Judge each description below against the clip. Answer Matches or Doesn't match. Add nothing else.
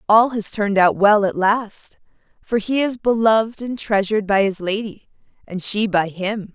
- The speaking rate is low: Doesn't match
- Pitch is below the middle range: Doesn't match